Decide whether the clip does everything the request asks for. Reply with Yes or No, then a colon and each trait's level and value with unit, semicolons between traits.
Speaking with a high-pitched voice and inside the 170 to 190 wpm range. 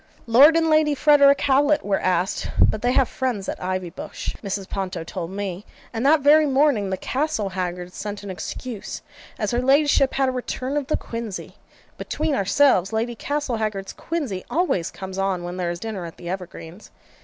Yes: high, 220 Hz; average, 175 wpm